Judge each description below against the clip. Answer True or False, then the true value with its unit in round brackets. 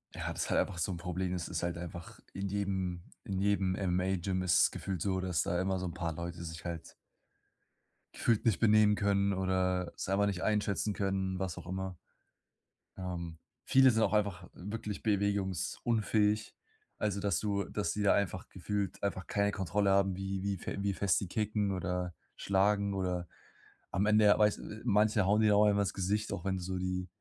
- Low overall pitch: True (95 Hz)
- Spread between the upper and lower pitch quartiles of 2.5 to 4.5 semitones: False (2.0 semitones)